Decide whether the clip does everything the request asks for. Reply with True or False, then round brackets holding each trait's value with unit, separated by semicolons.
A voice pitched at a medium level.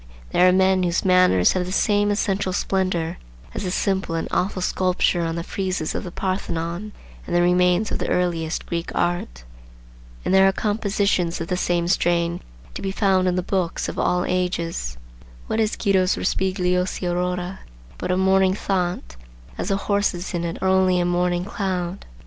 True (180 Hz)